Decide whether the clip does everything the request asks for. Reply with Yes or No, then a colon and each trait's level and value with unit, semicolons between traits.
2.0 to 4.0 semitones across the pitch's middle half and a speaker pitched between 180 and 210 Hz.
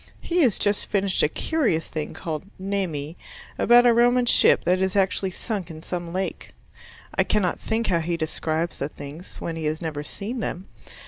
No: average, 4.6 semitones; medium, 185 Hz